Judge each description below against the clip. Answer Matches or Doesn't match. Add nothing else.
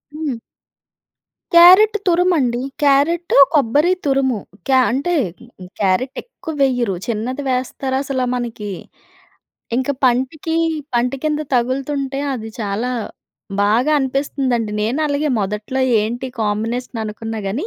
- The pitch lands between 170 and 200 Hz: Doesn't match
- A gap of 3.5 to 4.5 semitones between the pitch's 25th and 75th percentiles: Matches